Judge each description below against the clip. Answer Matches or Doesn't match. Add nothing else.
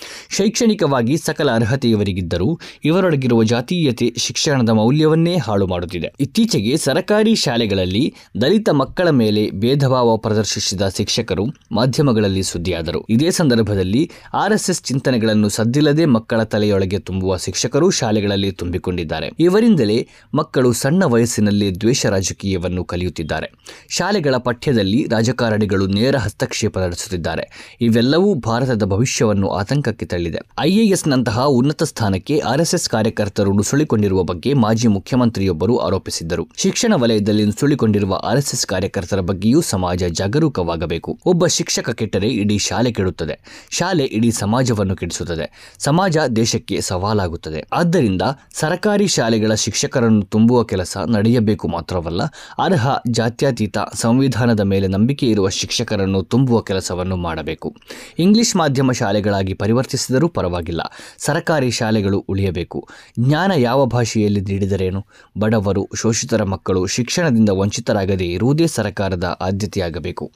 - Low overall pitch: Matches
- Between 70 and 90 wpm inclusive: Doesn't match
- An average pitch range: Doesn't match